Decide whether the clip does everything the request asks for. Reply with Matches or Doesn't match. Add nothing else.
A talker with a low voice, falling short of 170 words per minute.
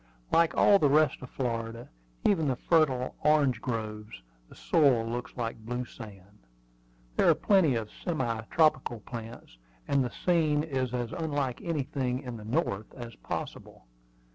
Matches